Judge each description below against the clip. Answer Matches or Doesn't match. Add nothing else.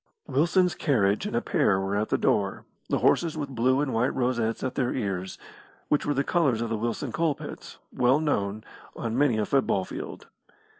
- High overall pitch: Doesn't match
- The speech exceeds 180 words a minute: Matches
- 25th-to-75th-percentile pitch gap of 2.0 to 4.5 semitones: Doesn't match